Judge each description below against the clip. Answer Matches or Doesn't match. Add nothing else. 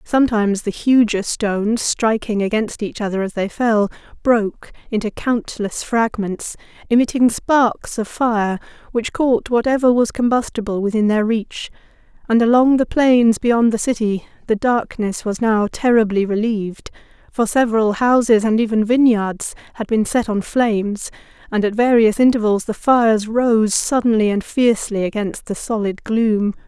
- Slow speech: Doesn't match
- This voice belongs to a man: Doesn't match